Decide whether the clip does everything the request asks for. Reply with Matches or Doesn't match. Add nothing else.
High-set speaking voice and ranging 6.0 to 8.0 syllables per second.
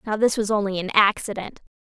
Matches